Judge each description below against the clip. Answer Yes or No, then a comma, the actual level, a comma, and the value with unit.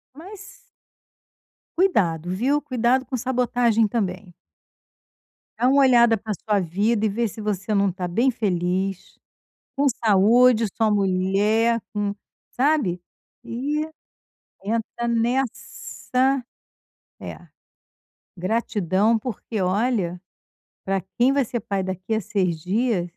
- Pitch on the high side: Yes, high, 220 Hz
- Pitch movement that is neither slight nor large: Yes, average, 4.4 semitones